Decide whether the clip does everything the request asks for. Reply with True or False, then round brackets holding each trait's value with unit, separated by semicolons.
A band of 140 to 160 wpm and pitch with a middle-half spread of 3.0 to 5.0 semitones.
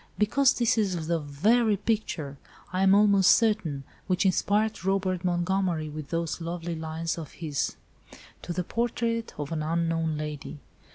True (150 wpm; 4.3 semitones)